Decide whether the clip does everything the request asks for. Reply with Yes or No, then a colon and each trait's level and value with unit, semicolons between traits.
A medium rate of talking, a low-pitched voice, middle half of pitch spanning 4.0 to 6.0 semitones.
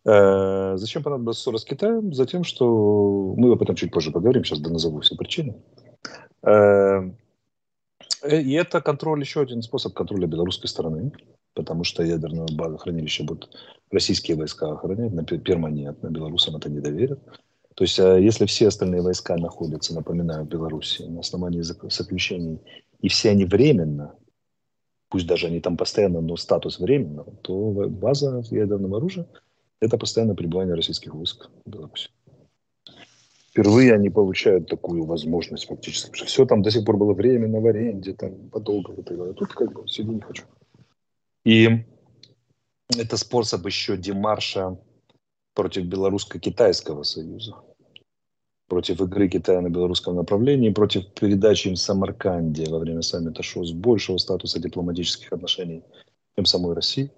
Yes: average, 135 wpm; very low, 95 Hz; average, 5.2 semitones